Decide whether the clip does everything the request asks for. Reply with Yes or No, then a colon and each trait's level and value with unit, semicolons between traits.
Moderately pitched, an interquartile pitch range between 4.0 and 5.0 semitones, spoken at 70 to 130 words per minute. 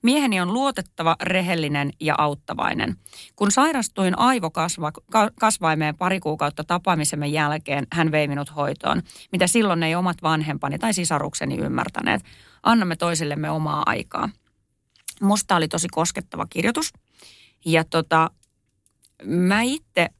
Yes: medium, 165 Hz; average, 4.7 semitones; average, 115 wpm